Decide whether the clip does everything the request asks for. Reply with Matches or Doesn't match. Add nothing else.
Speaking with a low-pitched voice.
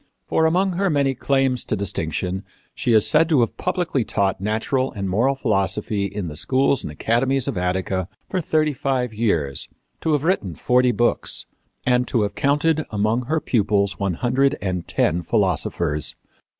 Matches